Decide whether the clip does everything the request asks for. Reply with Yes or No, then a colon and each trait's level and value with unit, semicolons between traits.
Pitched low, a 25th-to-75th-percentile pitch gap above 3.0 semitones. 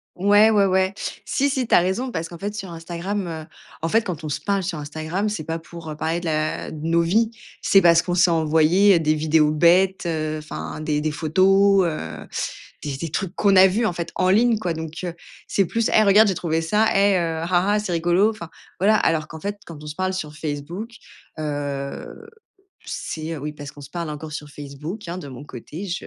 No: medium, 170 Hz; average, 4.0 semitones